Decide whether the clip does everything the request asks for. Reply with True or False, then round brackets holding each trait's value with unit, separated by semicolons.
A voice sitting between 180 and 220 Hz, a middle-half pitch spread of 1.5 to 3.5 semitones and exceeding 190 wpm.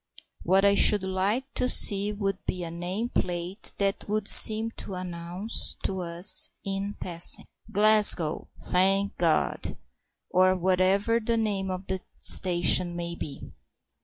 False (190 Hz; 2.5 semitones; 135 wpm)